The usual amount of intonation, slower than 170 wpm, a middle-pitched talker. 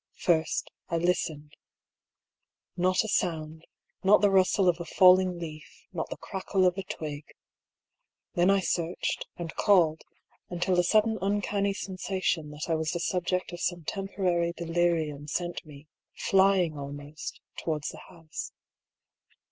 Yes: average, 3.0 semitones; average, 140 wpm; medium, 175 Hz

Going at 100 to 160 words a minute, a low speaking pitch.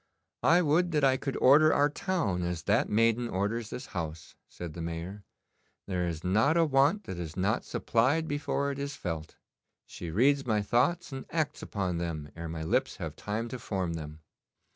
No: average, 185 wpm; low, 110 Hz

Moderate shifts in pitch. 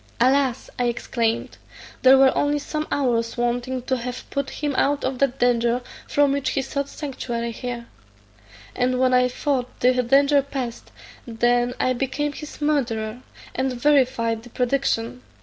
No: narrow, 2.3 semitones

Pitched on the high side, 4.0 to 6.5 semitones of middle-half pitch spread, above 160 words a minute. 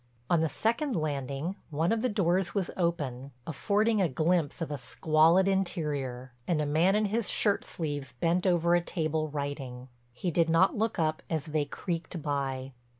No: medium, 165 Hz; average, 4.3 semitones; average, 175 wpm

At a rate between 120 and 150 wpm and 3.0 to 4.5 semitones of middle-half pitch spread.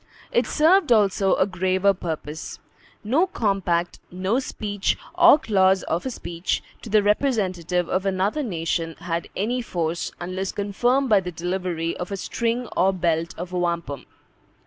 Yes: average, 145 wpm; average, 4.0 semitones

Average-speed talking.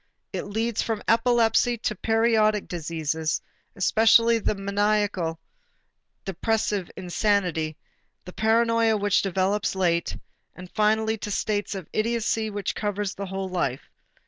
No: slow, 120 wpm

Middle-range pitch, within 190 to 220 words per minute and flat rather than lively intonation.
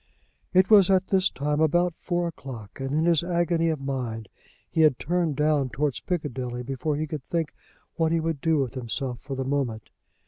No: medium, 150 Hz; average, 195 wpm; average, 4.1 semitones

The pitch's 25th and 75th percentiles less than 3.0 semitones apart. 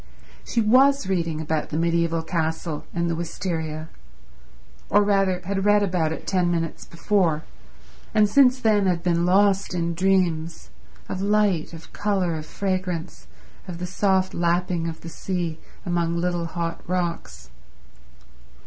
Yes: narrow, 2.6 semitones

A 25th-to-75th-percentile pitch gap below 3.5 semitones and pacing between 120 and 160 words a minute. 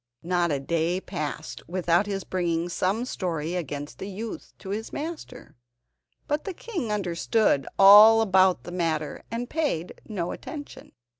No: average, 4.8 semitones; average, 145 wpm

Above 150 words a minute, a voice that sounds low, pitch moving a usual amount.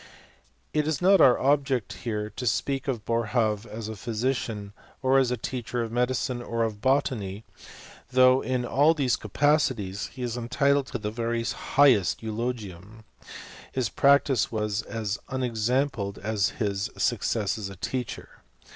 No: average, 145 wpm; low, 120 Hz; average, 3.6 semitones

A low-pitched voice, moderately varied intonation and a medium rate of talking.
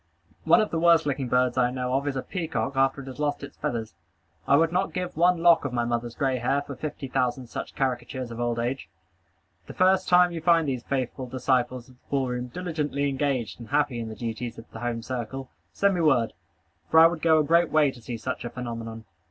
No: low, 130 Hz; average, 4.3 semitones; fast, 235 wpm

